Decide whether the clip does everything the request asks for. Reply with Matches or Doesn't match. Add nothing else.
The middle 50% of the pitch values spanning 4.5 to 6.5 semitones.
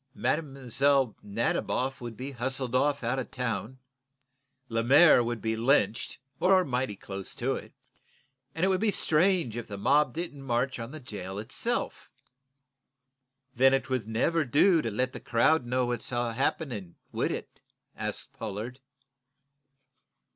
Doesn't match